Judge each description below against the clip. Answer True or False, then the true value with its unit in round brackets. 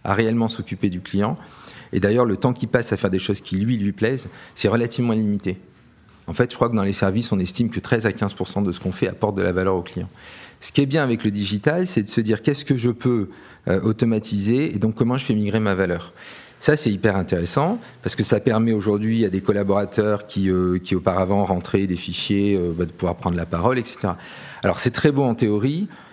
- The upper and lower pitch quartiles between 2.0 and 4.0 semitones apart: True (3.7 semitones)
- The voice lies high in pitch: False (105 Hz)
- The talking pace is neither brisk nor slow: False (235 wpm)